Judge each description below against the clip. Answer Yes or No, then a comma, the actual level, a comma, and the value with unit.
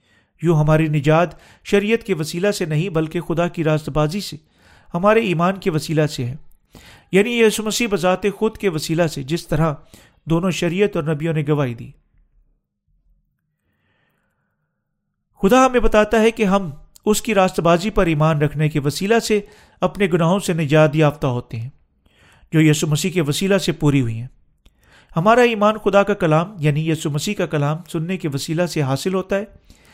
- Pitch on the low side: No, medium, 170 Hz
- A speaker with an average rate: Yes, average, 170 wpm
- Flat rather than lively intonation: No, average, 4.5 semitones